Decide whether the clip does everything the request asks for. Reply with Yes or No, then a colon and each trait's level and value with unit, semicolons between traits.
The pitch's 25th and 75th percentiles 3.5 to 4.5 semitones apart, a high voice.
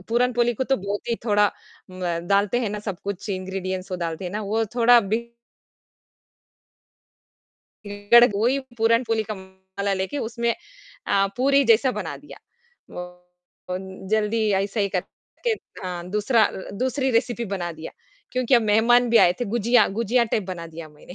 Yes: average, 4.0 semitones; high, 215 Hz